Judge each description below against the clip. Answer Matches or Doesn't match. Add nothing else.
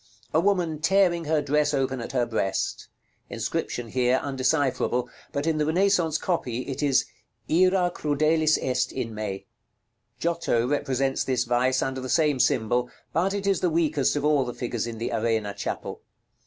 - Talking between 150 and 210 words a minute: Matches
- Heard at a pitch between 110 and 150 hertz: Matches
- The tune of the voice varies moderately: Matches